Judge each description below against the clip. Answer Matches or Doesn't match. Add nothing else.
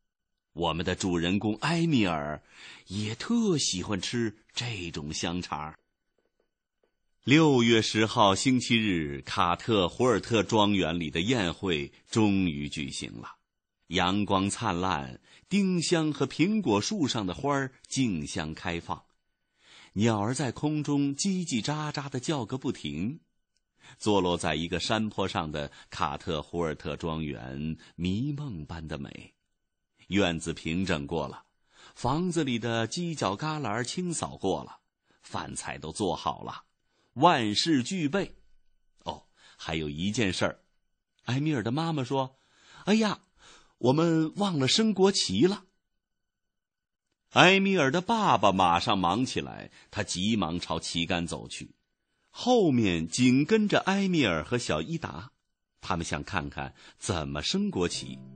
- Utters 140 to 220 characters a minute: Matches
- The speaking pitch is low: Matches